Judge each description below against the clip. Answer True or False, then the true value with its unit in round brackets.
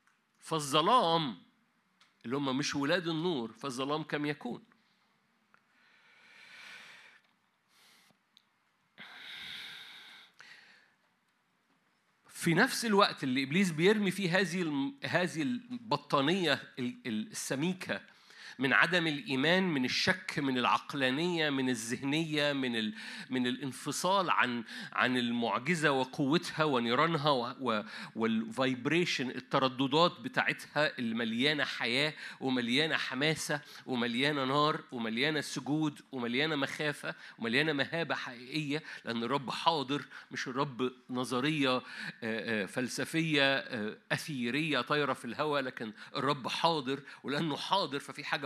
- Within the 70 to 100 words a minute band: True (90 wpm)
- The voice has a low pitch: False (145 Hz)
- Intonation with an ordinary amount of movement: True (4.1 semitones)